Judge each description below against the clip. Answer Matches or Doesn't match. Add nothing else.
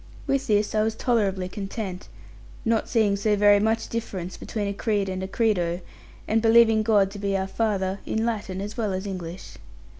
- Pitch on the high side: Matches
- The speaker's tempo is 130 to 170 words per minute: Doesn't match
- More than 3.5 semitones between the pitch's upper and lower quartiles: Doesn't match